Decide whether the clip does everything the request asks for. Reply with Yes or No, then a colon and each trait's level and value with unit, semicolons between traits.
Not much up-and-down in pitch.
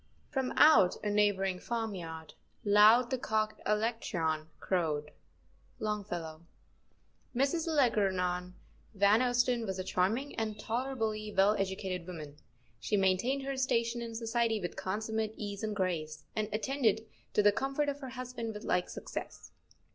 No: average, 4.1 semitones